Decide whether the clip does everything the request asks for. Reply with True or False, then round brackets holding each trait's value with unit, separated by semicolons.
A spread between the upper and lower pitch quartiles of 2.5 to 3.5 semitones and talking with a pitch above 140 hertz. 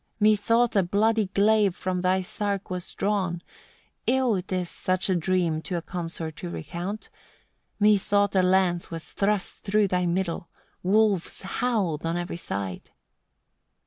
True (2.9 semitones; 185 Hz)